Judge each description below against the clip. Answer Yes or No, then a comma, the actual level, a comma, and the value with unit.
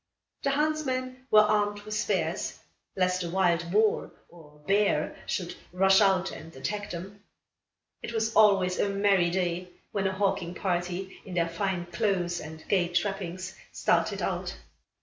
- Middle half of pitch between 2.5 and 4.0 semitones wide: Yes, average, 2.8 semitones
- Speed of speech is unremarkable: Yes, average, 150 wpm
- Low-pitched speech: No, high, 190 Hz